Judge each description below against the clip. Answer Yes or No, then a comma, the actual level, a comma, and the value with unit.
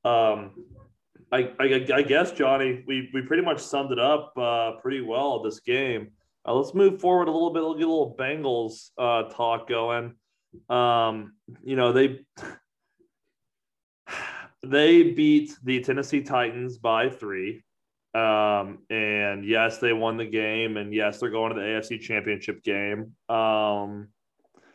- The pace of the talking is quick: No, average, 145 wpm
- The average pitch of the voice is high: No, low, 120 Hz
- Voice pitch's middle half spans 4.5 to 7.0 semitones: No, average, 3.5 semitones